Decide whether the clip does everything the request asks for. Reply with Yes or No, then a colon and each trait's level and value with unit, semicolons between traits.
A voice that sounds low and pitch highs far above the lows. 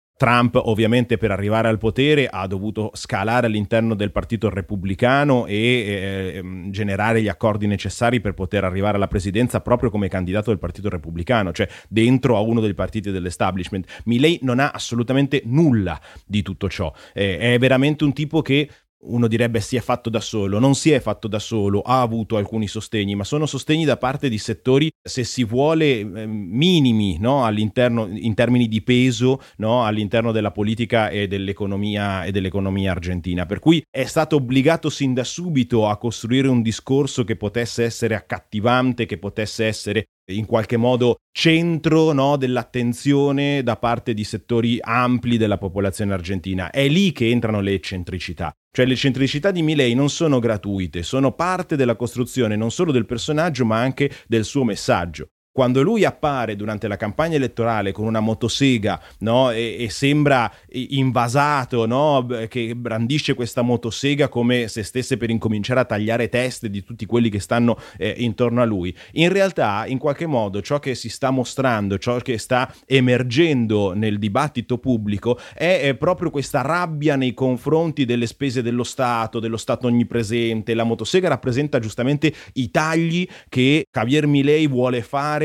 No: low, 120 Hz; average, 3.9 semitones